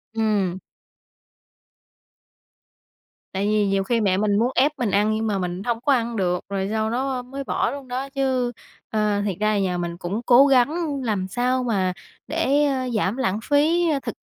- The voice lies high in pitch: Yes, high, 225 Hz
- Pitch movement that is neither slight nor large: Yes, average, 4.9 semitones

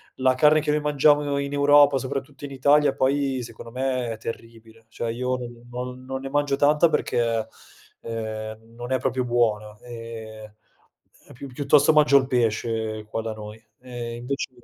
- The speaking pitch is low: Yes, low, 125 Hz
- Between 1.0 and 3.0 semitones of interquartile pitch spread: No, average, 3.6 semitones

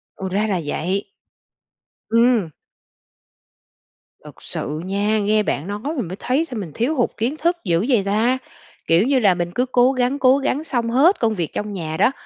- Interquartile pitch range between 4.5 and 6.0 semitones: Yes, average, 5.0 semitones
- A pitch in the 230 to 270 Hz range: No, high, 220 Hz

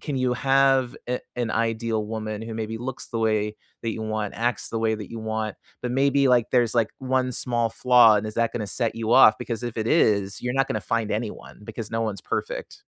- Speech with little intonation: Yes, narrow, 2.2 semitones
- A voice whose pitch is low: Yes, low, 115 Hz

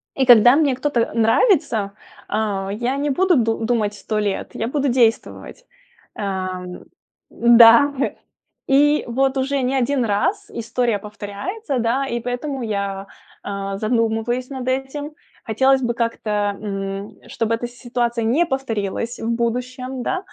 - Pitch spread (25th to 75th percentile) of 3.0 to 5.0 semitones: Yes, average, 3.5 semitones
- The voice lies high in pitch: Yes, high, 240 Hz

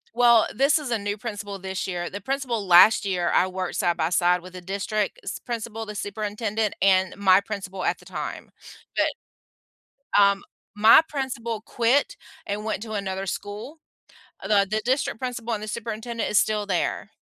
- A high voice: Yes, high, 210 Hz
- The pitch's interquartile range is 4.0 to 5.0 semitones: No, average, 3.2 semitones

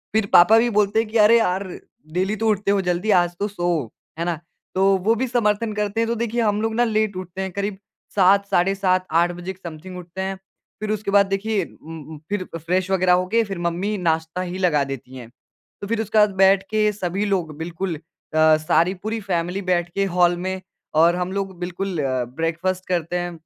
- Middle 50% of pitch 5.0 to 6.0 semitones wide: No, average, 3.0 semitones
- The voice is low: No, high, 190 Hz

